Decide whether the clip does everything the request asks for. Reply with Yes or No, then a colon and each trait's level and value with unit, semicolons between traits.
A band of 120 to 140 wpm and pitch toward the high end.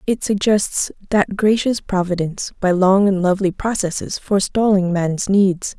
Yes: slow, 135 wpm; high, 195 Hz